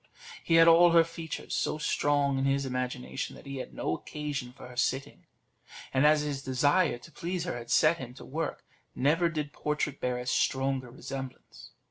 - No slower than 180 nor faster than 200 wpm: Yes, average, 185 wpm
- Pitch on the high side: No, medium, 140 Hz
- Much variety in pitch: No, average, 3.4 semitones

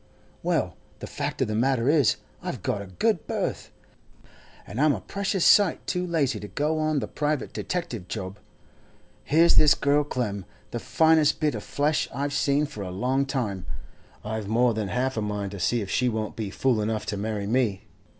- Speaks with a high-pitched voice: No, low, 125 Hz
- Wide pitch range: Yes, wide, 6.0 semitones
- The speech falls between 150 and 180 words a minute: No, average, 190 wpm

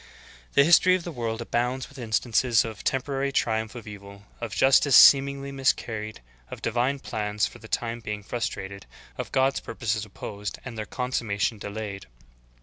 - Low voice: Yes, low, 115 Hz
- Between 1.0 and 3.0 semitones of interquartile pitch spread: No, average, 3.8 semitones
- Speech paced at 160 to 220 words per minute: Yes, average, 170 wpm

